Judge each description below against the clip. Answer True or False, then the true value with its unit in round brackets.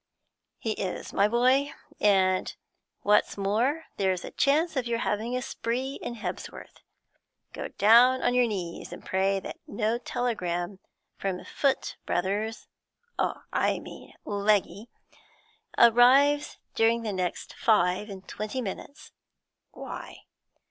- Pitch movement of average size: True (4.1 semitones)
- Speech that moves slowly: True (120 wpm)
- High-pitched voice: True (220 Hz)